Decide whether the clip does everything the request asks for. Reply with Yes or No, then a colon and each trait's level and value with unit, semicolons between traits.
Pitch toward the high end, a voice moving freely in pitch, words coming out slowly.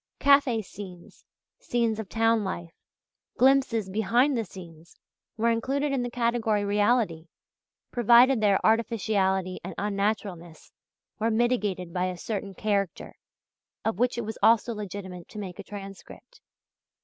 No: high, 215 Hz; average, 3.6 semitones; slow, 130 wpm